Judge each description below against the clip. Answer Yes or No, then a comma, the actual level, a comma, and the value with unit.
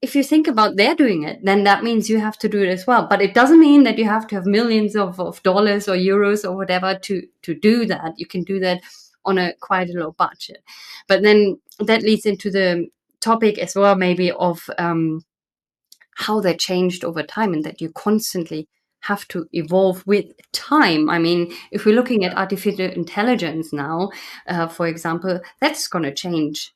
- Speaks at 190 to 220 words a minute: Yes, average, 200 wpm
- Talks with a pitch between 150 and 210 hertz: Yes, high, 190 Hz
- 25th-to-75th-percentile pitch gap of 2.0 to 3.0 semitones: No, average, 3.5 semitones